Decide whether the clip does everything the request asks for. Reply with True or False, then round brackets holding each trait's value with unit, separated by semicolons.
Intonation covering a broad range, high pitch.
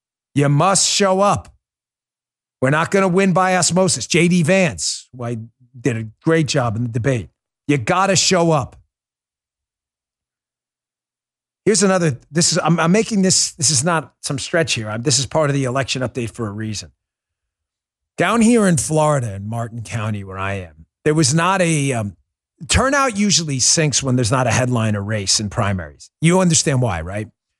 False (7.7 semitones; 135 Hz)